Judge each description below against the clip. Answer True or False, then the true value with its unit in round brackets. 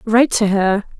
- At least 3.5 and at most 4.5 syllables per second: False (4.9 syllables/s)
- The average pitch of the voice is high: True (215 Hz)